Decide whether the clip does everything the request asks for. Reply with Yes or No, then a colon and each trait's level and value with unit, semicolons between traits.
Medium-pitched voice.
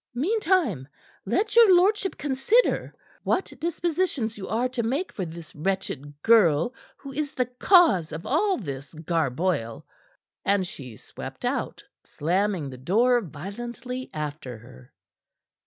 No: high, 215 Hz